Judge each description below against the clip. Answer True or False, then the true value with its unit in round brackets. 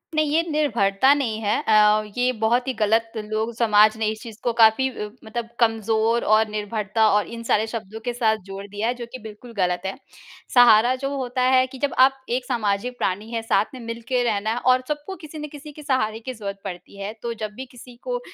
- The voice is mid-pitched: False (230 Hz)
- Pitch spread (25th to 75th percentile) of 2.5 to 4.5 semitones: True (2.9 semitones)